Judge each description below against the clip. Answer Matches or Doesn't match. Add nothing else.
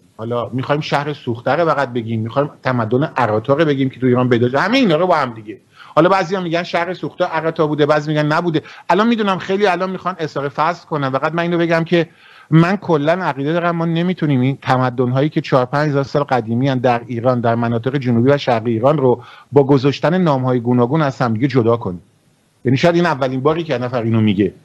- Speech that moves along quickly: Matches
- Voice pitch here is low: Doesn't match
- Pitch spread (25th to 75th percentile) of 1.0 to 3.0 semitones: Doesn't match